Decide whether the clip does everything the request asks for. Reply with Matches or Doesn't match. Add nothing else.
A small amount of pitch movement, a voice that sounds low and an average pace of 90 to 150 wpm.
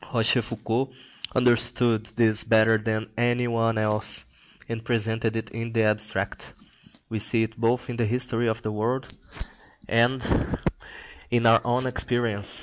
Matches